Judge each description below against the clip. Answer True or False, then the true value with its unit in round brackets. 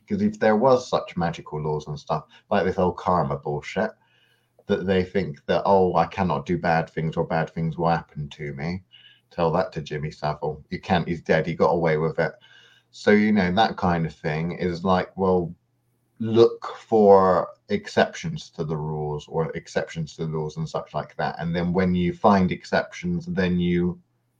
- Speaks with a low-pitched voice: True (90 Hz)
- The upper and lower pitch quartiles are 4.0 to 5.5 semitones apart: True (4.5 semitones)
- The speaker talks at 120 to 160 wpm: False (190 wpm)